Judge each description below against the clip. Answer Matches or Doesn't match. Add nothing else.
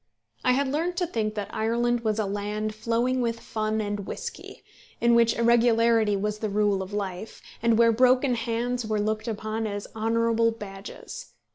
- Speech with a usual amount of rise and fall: Doesn't match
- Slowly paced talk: Doesn't match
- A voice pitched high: Matches